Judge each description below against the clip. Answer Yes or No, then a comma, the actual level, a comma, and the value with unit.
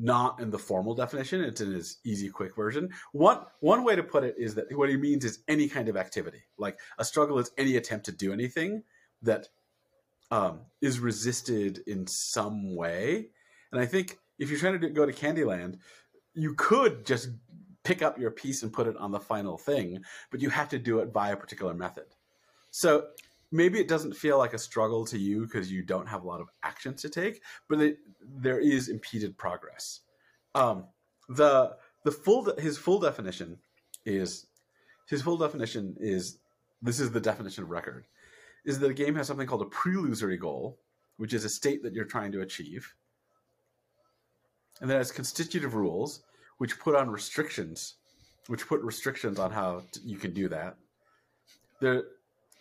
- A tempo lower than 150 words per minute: No, average, 185 wpm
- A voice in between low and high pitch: No, low, 125 Hz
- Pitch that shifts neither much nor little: No, wide, 5.8 semitones